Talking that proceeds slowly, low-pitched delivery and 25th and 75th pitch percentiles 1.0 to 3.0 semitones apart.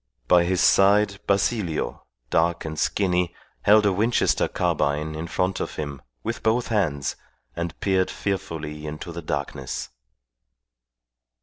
No: slow, 125 wpm; very low, 85 Hz; average, 4.3 semitones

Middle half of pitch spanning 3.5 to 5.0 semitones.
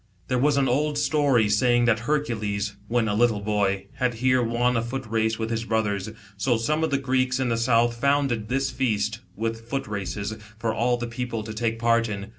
No: average, 2.7 semitones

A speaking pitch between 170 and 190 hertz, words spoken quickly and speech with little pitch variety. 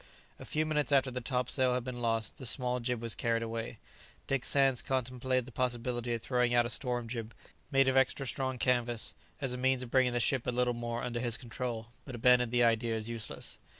No: low, 125 Hz; fast, 215 wpm; narrow, 1.6 semitones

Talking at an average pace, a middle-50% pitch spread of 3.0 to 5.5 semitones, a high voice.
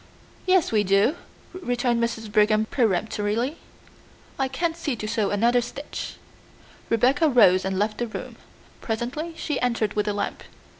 Yes: average, 145 wpm; average, 4.0 semitones; high, 230 Hz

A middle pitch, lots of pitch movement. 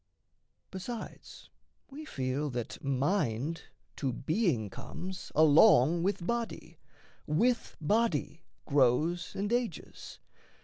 Yes: medium, 165 Hz; wide, 6.9 semitones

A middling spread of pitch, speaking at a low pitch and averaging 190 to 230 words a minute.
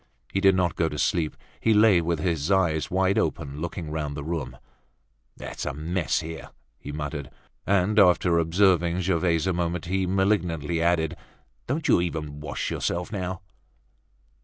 No: average, 3.0 semitones; very low, 85 Hz; average, 160 wpm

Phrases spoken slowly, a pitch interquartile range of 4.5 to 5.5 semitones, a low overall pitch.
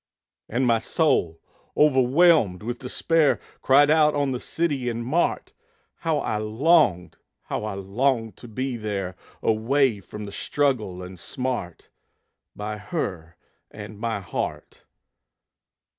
Yes: slow, 125 wpm; average, 5.2 semitones; low, 115 Hz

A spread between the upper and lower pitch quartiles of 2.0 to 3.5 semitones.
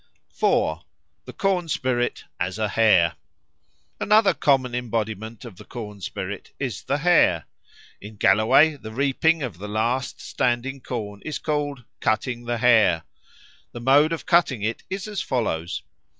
No: average, 4.8 semitones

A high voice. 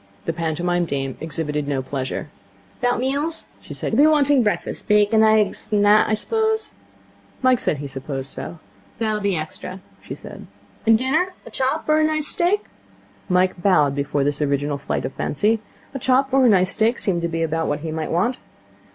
Yes: high, 195 Hz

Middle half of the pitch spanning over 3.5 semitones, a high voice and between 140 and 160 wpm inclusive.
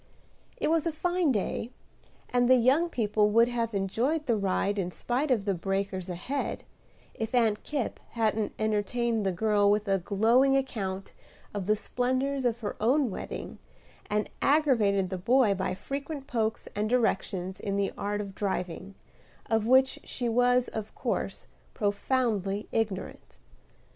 Yes: average, 4.1 semitones; high, 220 Hz; average, 150 wpm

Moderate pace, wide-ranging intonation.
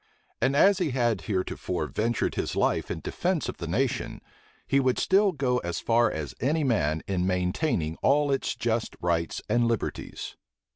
Yes: average, 165 wpm; wide, 7.2 semitones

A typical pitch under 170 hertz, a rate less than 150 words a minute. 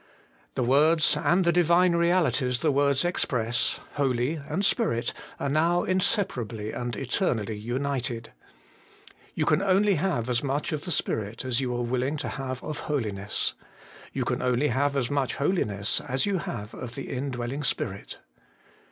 No: low, 135 Hz; average, 155 wpm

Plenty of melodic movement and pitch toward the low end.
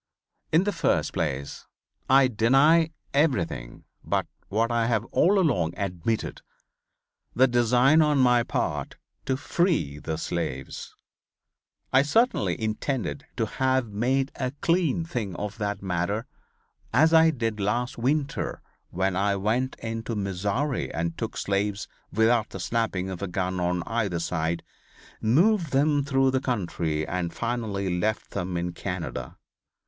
Yes: wide, 6.2 semitones; low, 115 Hz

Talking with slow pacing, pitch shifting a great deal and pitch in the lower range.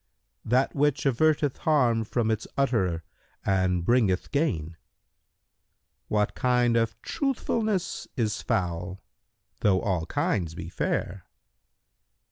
Yes: slow, 105 wpm; wide, 6.8 semitones; low, 115 Hz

